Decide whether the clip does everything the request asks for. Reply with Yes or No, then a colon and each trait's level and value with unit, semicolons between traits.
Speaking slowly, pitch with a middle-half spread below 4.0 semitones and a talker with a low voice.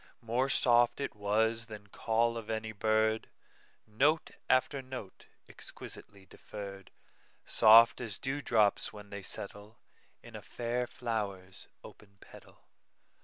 Yes: slow, 110 wpm; average, 2.7 semitones; low, 110 Hz